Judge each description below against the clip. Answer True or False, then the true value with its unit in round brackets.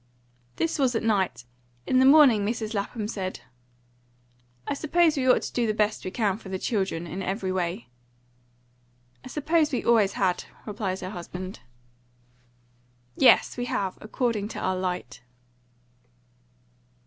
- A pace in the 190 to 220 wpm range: False (145 wpm)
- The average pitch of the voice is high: True (210 Hz)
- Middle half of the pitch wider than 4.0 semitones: True (4.8 semitones)